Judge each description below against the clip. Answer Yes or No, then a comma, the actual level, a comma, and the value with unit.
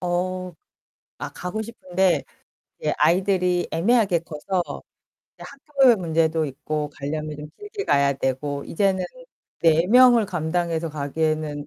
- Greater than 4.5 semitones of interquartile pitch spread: No, average, 3.7 semitones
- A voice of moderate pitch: Yes, medium, 170 Hz